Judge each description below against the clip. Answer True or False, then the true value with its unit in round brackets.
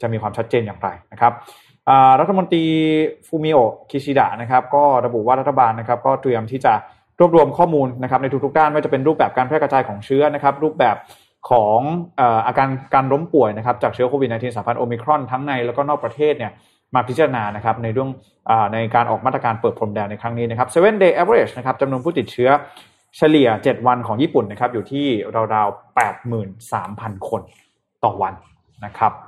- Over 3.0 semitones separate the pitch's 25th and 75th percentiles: True (3.9 semitones)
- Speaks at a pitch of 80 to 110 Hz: False (130 Hz)